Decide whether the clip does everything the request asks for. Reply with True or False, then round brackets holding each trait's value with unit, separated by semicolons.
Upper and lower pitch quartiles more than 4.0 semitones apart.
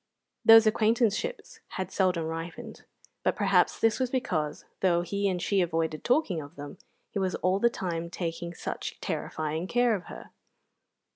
True (4.8 semitones)